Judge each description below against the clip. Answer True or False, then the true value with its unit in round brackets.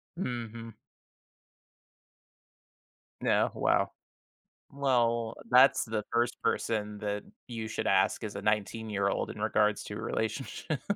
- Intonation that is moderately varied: False (2.0 semitones)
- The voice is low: True (110 Hz)